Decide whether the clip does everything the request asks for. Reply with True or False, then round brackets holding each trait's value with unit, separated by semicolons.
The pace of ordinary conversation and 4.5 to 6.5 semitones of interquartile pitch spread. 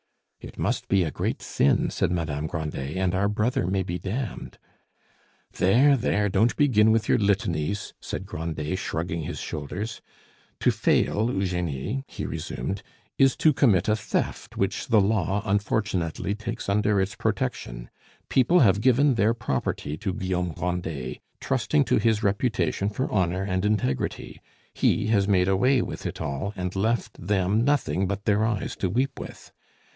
False (155 wpm; 3.7 semitones)